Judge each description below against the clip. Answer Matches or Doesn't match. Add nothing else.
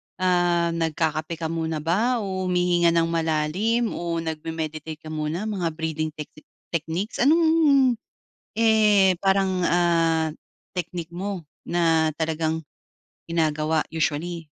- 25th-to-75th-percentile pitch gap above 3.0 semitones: Doesn't match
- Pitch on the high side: Doesn't match